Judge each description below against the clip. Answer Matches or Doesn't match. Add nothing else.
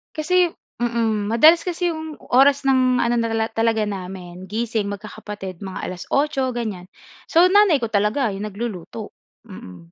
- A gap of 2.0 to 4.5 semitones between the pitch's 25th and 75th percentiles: Doesn't match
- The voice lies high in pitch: Matches